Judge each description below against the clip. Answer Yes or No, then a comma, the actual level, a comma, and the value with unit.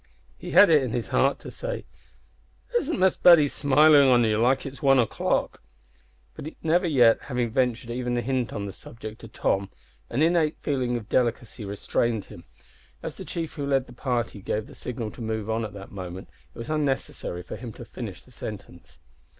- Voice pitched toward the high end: No, low, 125 Hz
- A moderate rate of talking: Yes, average, 190 wpm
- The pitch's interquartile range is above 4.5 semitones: No, average, 4.2 semitones